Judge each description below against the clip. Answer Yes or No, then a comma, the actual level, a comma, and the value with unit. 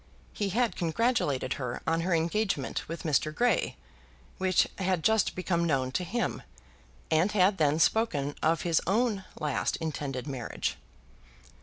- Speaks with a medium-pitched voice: Yes, medium, 170 Hz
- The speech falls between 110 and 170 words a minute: Yes, average, 140 wpm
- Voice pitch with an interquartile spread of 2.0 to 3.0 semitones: No, average, 4.8 semitones